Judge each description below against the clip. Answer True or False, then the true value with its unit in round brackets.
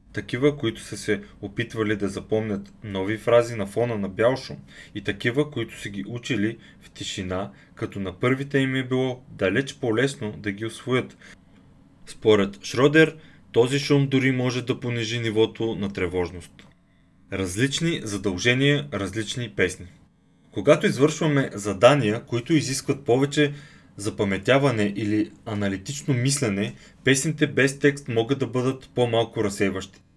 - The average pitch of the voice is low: True (115 Hz)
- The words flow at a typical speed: True (130 wpm)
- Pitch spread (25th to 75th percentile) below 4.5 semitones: False (5.2 semitones)